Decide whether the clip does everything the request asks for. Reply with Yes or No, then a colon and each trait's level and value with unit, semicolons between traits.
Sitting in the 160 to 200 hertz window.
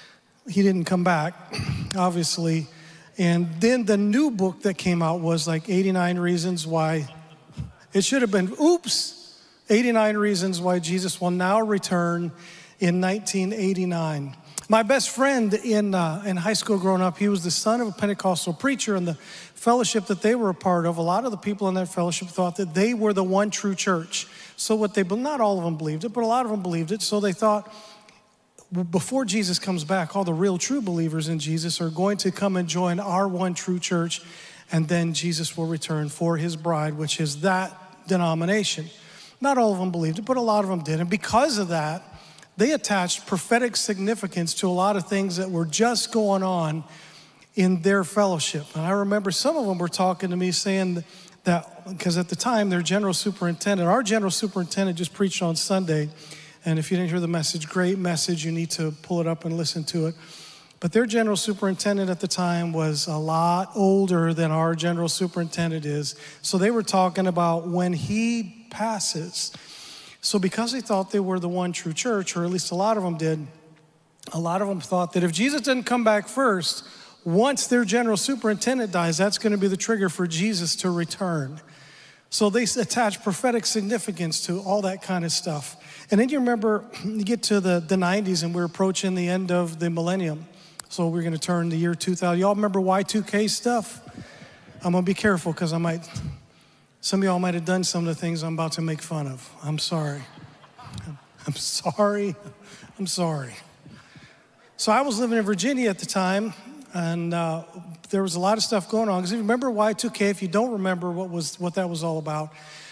Yes: medium, 185 Hz